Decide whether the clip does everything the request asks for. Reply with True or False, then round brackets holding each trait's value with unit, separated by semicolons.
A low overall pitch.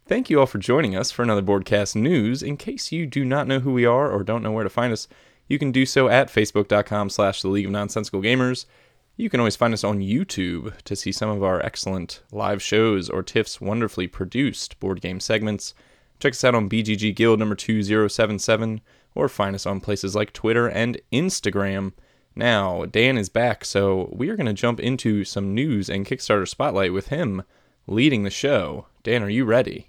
True (105 Hz)